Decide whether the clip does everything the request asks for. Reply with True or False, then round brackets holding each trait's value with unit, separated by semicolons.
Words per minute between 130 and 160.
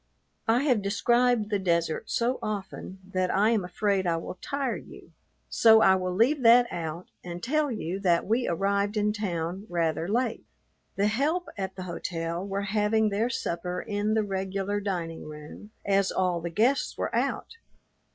False (170 wpm)